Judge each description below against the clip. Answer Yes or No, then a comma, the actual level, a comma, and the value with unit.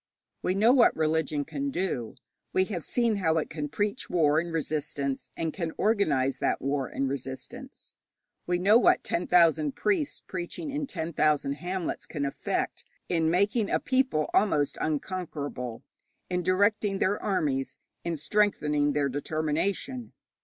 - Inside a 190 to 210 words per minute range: No, average, 145 wpm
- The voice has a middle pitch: Yes, medium, 165 Hz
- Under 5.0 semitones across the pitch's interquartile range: No, wide, 5.5 semitones